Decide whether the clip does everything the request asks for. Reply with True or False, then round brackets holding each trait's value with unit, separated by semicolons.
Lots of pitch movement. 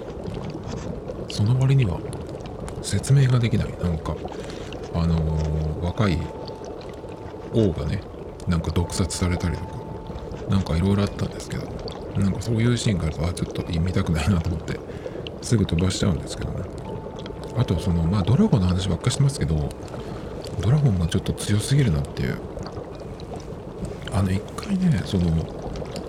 False (4.7 semitones)